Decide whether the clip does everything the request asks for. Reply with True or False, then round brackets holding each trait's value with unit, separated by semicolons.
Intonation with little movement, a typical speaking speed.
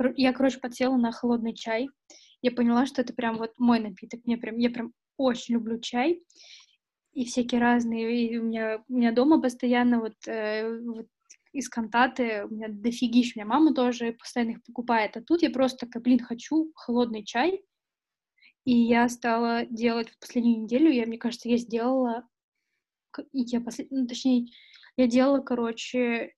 False (1.6 semitones; 170 wpm)